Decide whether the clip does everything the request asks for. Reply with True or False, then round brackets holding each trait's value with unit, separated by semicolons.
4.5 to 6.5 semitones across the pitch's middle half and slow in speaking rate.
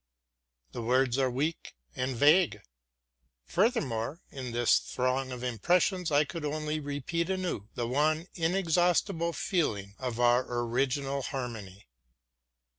True (5.2 semitones; 115 wpm)